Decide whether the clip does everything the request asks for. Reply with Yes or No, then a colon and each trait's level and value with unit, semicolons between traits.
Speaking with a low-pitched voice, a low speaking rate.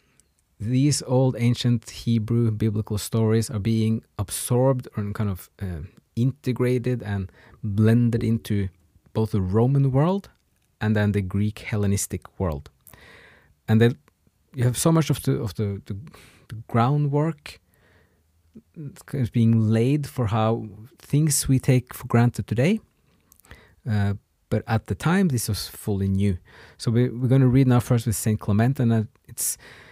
No: low, 115 Hz; average, 150 wpm